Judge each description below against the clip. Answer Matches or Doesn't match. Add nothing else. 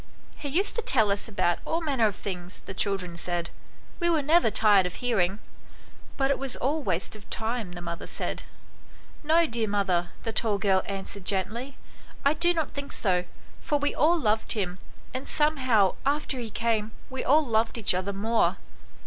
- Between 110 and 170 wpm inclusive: Doesn't match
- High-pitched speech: Matches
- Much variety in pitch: Matches